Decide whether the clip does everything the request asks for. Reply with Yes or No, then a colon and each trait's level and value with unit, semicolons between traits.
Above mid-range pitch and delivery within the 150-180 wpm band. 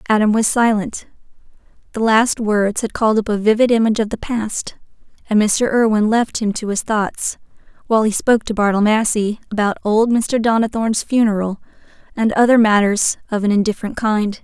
Yes: high, 215 Hz; average, 170 wpm